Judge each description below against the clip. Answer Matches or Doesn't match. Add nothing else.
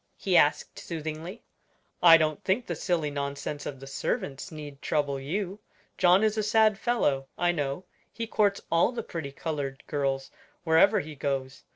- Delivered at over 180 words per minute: Doesn't match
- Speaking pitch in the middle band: Matches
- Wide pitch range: Matches